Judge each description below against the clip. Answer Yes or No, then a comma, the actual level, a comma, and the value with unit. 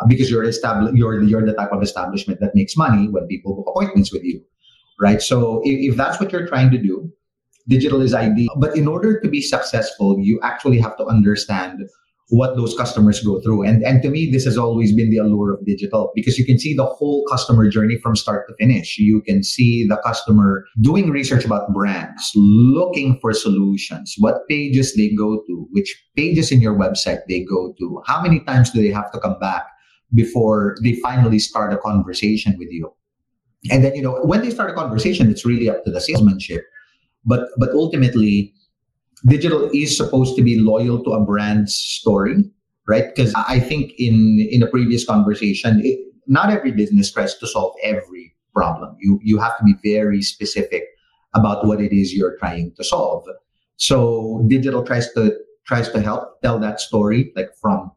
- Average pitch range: Yes, average, 4.2 semitones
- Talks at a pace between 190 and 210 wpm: Yes, average, 195 wpm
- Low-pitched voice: Yes, low, 115 Hz